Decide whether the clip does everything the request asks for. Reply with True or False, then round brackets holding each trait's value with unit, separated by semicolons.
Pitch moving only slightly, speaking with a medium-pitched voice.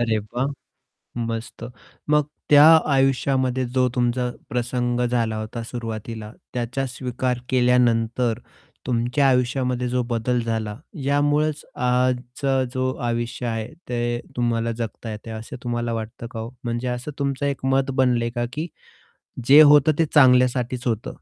False (1.9 semitones; 125 Hz)